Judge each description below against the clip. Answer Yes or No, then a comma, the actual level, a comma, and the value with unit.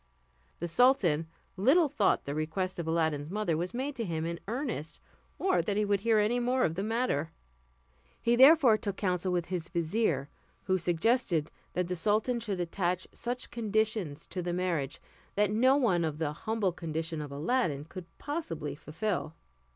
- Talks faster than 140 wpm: Yes, average, 170 wpm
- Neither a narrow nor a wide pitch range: No, wide, 5.8 semitones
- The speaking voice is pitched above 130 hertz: Yes, medium, 185 Hz